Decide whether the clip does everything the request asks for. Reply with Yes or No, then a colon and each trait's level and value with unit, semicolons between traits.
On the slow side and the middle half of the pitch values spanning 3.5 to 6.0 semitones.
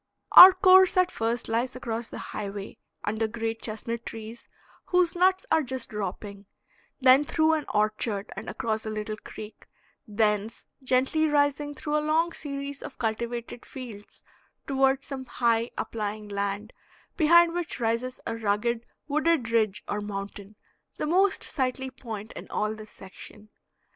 No: average, 145 wpm; average, 5.1 semitones